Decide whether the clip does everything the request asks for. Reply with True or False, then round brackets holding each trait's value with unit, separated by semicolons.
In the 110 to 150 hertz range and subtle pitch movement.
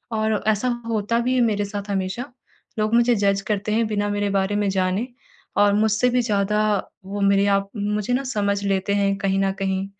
False (205 Hz; 1.7 semitones)